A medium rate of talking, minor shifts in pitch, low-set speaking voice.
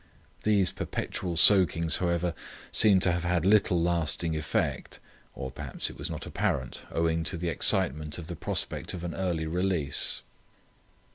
Yes: average, 150 wpm; narrow, 2.0 semitones; very low, 85 Hz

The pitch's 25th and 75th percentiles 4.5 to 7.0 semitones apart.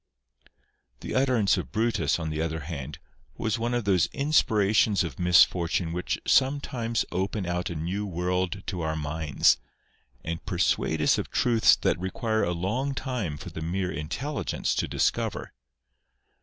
Yes: wide, 5.5 semitones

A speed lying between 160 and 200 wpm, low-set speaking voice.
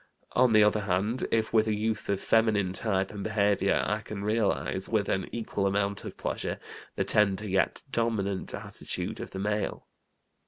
Yes: average, 170 wpm; low, 105 Hz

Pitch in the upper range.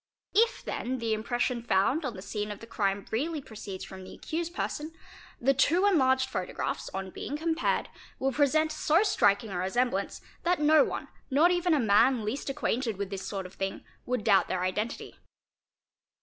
Yes: very high, 250 Hz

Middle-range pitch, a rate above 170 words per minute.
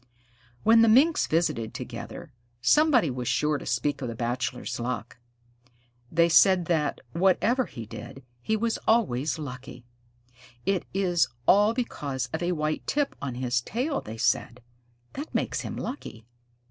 No: medium, 155 Hz; average, 145 wpm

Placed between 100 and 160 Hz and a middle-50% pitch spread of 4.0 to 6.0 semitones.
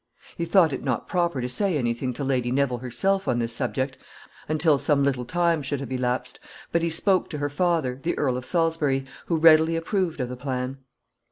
Yes: medium, 140 Hz; average, 4.6 semitones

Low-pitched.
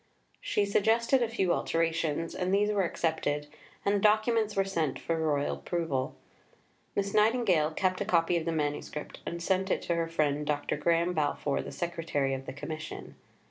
No: medium, 170 Hz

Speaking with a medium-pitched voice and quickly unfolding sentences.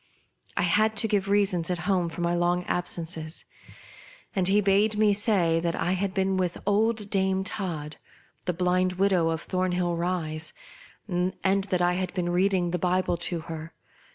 No: medium, 180 Hz; average, 170 wpm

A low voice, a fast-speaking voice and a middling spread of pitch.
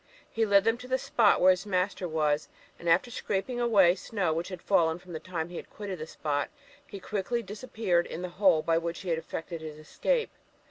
No: medium, 185 Hz; fast, 225 wpm; average, 4.0 semitones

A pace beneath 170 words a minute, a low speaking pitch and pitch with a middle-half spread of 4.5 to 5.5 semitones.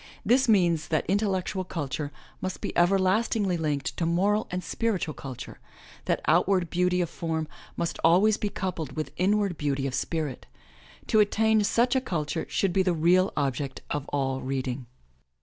No: average, 160 wpm; medium, 175 Hz; average, 4.9 semitones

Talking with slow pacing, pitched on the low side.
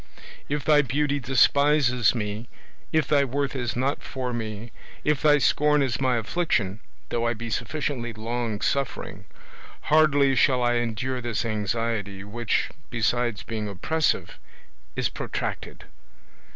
Yes: slow, 130 wpm; low, 120 Hz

